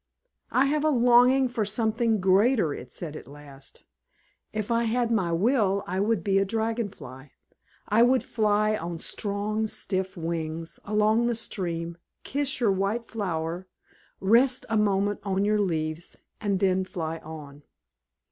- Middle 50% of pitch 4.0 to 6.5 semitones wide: Yes, average, 5.0 semitones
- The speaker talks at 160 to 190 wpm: No, average, 150 wpm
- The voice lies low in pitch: No, high, 205 Hz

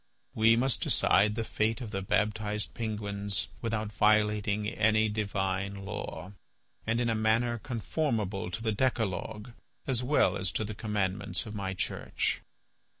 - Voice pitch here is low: Yes, low, 105 Hz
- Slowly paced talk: No, average, 145 wpm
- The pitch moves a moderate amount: No, narrow, 2.0 semitones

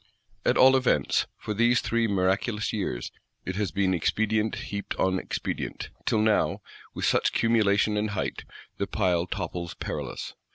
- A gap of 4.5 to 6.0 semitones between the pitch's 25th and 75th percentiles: No, average, 2.8 semitones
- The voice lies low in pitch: Yes, low, 105 Hz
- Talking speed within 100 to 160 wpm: Yes, average, 150 wpm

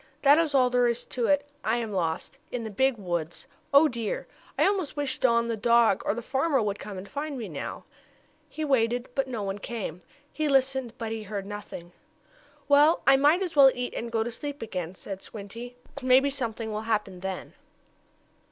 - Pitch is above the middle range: Yes, high, 235 Hz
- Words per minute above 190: Yes, average, 200 wpm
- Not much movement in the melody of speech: No, average, 4.6 semitones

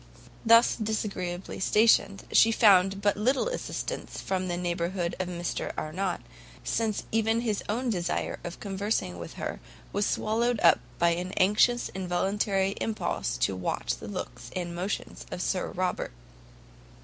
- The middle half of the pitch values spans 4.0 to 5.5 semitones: No, average, 3.6 semitones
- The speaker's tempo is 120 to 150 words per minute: Yes, average, 145 wpm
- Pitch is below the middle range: No, high, 195 Hz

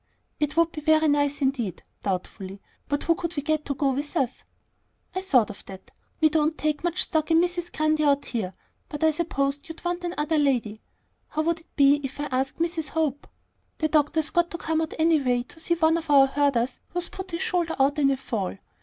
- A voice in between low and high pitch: No, very high, 300 Hz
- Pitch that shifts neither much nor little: Yes, average, 3.1 semitones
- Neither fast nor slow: No, fast, 215 wpm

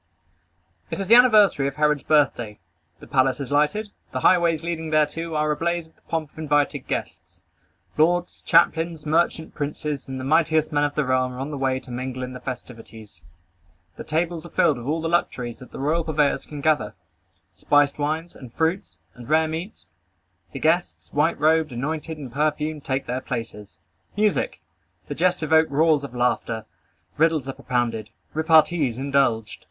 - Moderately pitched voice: Yes, medium, 150 Hz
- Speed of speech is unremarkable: Yes, average, 175 wpm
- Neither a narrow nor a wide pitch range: Yes, average, 3.7 semitones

